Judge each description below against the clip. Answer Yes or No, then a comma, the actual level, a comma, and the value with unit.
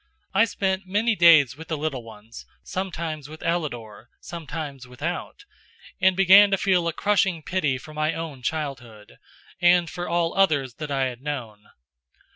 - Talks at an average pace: Yes, average, 155 wpm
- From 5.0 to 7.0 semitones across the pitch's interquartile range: Yes, wide, 5.4 semitones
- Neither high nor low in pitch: Yes, medium, 160 Hz